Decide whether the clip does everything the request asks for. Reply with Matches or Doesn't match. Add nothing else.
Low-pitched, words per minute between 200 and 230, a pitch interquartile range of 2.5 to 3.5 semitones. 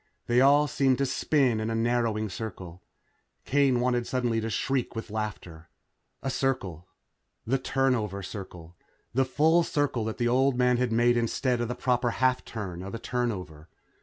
Doesn't match